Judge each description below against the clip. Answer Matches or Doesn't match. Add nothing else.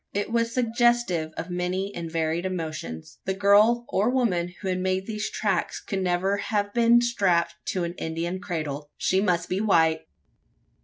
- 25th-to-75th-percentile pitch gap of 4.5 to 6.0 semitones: Doesn't match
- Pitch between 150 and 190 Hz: Matches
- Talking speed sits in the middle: Matches